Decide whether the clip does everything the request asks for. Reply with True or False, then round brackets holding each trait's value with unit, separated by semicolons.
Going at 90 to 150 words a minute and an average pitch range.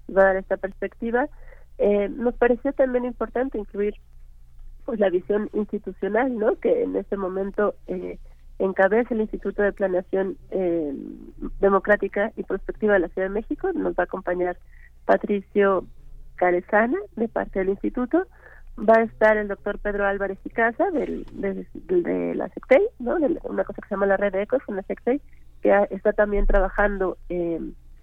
False (170 wpm; 3.2 semitones)